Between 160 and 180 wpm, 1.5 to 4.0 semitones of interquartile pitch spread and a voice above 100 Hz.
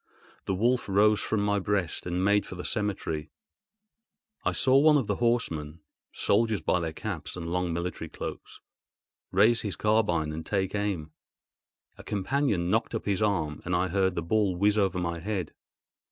No: average, 175 wpm; average, 3.6 semitones; very low, 95 Hz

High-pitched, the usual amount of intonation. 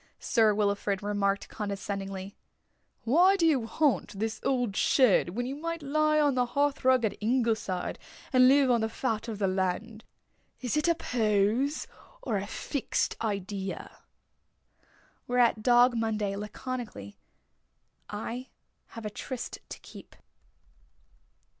Yes: high, 225 Hz; average, 4.2 semitones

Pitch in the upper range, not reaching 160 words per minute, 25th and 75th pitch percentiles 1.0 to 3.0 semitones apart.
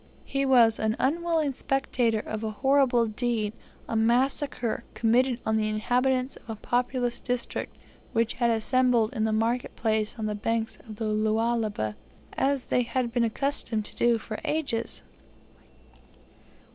Yes: high, 235 Hz; average, 145 wpm; average, 2.7 semitones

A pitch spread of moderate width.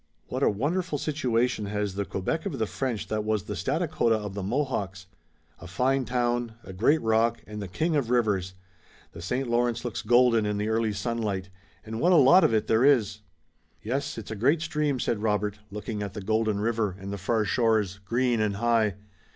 Yes: average, 3.4 semitones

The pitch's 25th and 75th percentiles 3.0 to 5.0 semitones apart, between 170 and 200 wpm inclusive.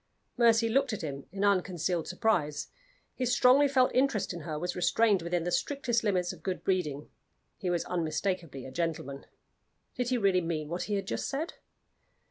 No: wide, 5.6 semitones; average, 175 wpm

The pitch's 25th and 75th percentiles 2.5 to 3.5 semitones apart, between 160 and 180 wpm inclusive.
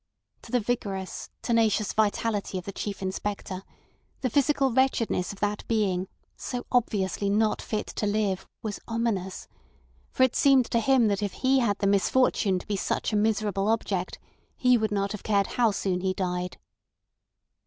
Yes: average, 2.9 semitones; average, 165 wpm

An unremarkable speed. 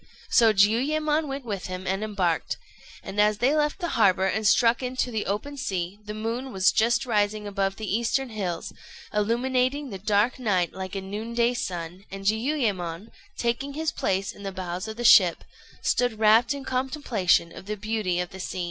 Yes: average, 185 wpm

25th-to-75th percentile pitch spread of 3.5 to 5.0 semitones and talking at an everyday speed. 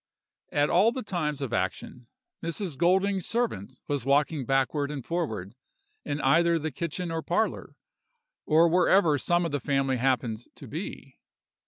Yes: average, 4.3 semitones; average, 150 wpm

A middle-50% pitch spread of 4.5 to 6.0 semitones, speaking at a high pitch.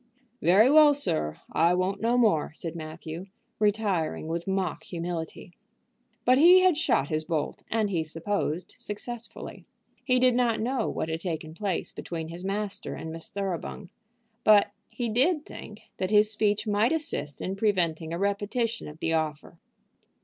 Yes: wide, 5.4 semitones; high, 195 Hz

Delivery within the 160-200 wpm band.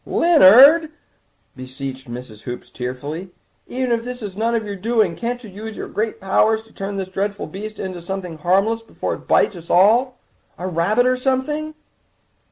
Yes: average, 170 wpm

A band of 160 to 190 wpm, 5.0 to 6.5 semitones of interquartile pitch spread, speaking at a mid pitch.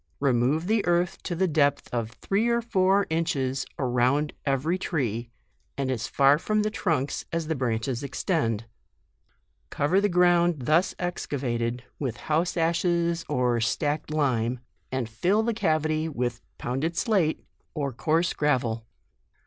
No: average, 150 wpm; wide, 5.6 semitones; medium, 150 Hz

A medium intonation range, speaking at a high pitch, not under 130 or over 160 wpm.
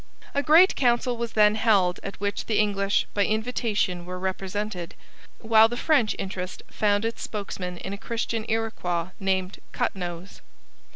Yes: average, 3.1 semitones; high, 205 Hz; average, 155 wpm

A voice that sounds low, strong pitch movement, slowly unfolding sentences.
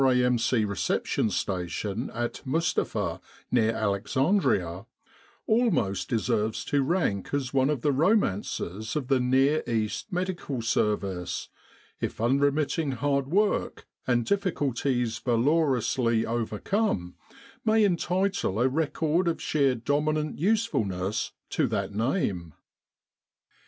Yes: low, 130 Hz; wide, 6.0 semitones; slow, 105 wpm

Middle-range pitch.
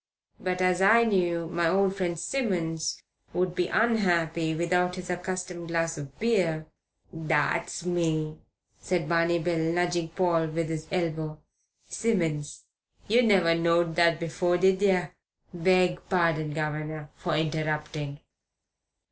Yes: medium, 170 Hz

